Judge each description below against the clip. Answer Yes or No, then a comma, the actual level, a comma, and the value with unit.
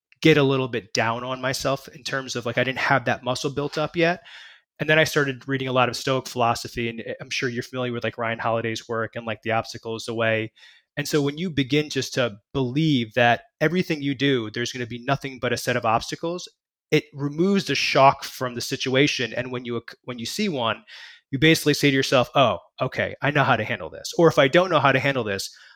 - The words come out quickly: Yes, fast, 240 wpm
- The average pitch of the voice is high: No, low, 130 Hz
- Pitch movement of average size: Yes, average, 3.3 semitones